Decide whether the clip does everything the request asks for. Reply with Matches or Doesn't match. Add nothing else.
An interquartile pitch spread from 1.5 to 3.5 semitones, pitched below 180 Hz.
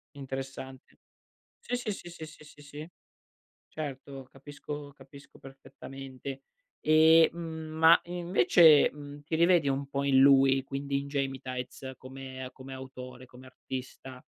Matches